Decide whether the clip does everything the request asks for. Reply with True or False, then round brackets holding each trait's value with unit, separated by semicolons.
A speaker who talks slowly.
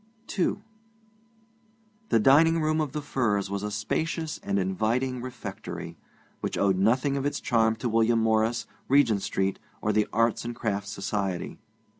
False (150 wpm)